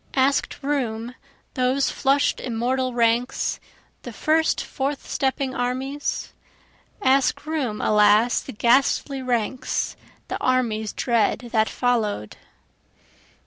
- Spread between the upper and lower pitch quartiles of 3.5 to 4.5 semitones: No, average, 2.8 semitones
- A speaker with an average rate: No, slow, 100 wpm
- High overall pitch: Yes, very high, 255 Hz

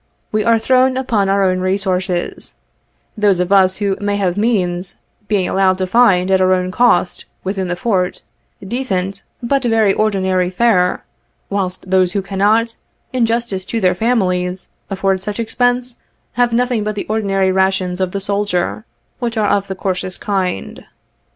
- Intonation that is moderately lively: Yes, average, 3.2 semitones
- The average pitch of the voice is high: Yes, high, 195 Hz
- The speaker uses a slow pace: No, average, 165 wpm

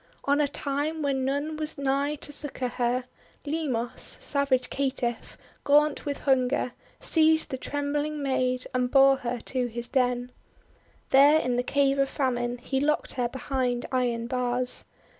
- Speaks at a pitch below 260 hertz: No, very high, 270 Hz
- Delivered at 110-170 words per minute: Yes, average, 150 wpm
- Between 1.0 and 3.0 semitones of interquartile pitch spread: Yes, narrow, 2.5 semitones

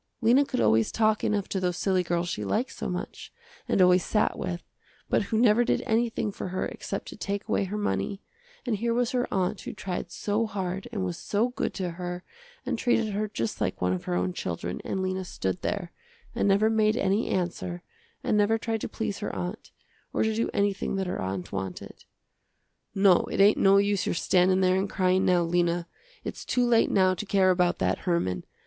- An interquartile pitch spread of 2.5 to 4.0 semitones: Yes, average, 3.3 semitones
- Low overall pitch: No, high, 190 Hz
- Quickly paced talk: Yes, fast, 210 wpm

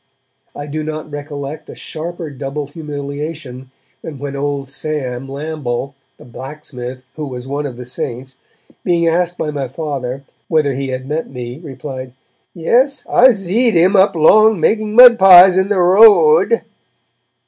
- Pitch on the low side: No, medium, 150 Hz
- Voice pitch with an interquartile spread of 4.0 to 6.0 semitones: Yes, average, 4.6 semitones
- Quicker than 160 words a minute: No, average, 155 wpm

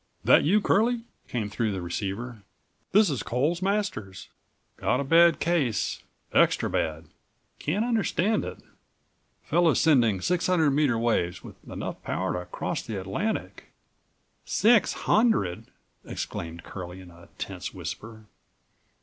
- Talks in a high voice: No, low, 125 Hz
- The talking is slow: Yes, slow, 125 wpm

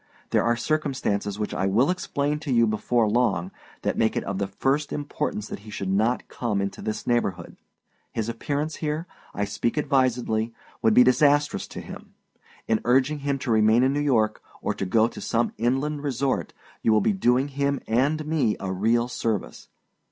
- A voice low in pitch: Yes, low, 120 Hz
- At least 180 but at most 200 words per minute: Yes, average, 185 wpm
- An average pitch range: Yes, average, 4.7 semitones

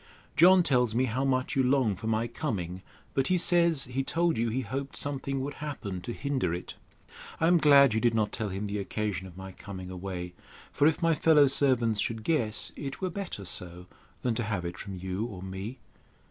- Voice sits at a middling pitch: No, low, 120 Hz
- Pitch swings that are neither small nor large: No, wide, 6.0 semitones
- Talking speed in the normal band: No, fast, 210 wpm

